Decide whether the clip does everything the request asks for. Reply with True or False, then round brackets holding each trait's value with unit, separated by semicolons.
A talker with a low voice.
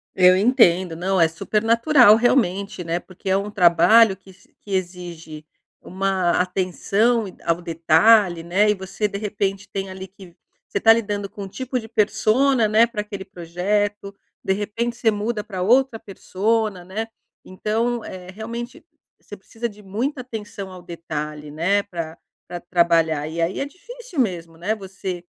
False (195 Hz)